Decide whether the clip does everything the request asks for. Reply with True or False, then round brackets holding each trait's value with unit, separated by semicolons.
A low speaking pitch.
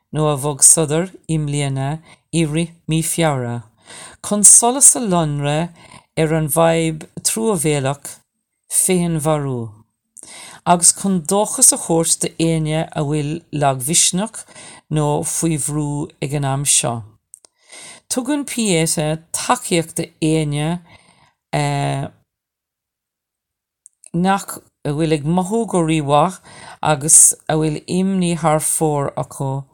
False (160 Hz)